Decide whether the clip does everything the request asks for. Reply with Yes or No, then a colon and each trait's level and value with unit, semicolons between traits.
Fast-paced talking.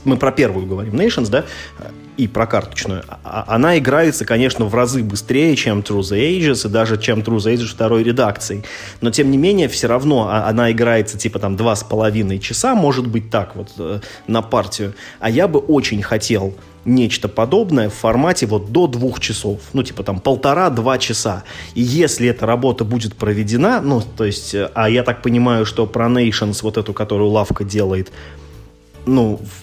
Yes: fast, 175 wpm